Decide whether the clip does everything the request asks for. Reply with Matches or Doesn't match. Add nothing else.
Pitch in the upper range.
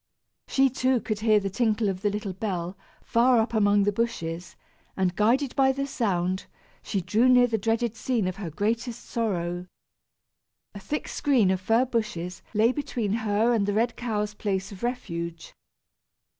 Matches